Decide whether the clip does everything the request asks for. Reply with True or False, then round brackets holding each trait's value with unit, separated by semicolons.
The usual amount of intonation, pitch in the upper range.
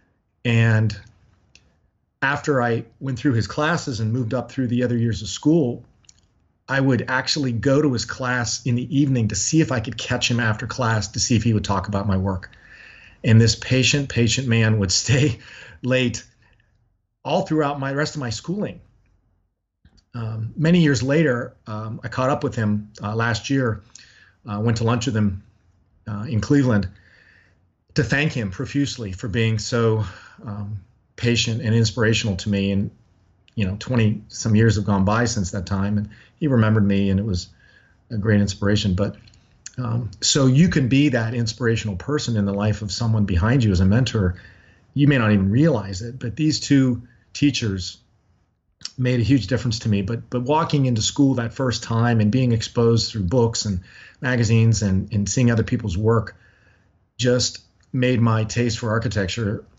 False (3.4 semitones; 115 Hz)